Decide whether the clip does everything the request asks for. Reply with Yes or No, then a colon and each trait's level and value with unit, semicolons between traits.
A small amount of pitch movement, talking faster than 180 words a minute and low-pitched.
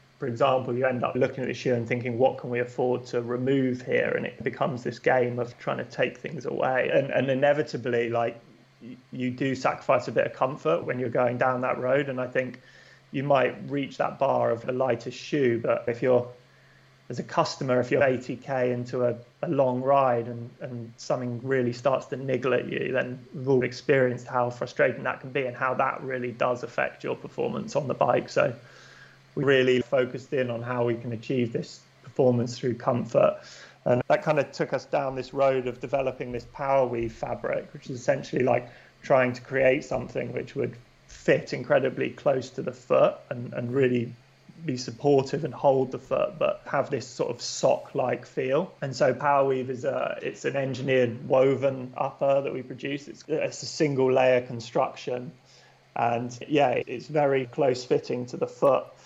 Yes: narrow, 1.8 semitones; average, 195 wpm; low, 130 Hz